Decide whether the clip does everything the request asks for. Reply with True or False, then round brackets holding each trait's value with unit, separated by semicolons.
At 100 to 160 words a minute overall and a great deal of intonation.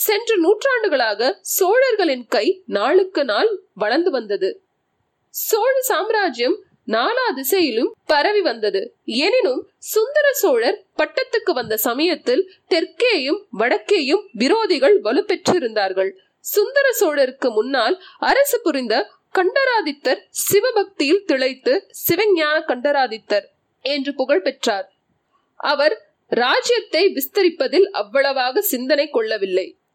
False (85 wpm; 7.5 semitones)